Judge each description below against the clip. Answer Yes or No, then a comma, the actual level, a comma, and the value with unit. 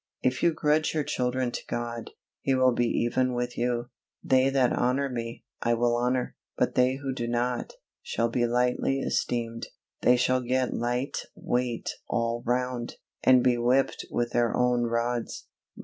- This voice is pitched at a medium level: No, low, 125 Hz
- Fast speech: No, average, 165 wpm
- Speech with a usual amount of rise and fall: No, narrow, 1.3 semitones